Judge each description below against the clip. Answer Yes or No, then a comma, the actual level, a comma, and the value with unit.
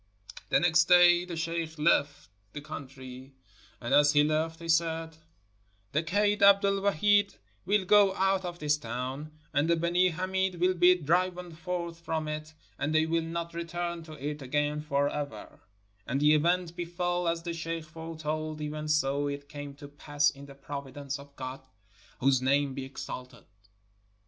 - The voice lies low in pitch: No, medium, 155 Hz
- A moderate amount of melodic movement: Yes, average, 3.3 semitones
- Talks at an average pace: Yes, average, 170 wpm